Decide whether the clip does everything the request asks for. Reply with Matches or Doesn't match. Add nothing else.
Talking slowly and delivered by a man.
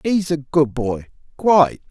Matches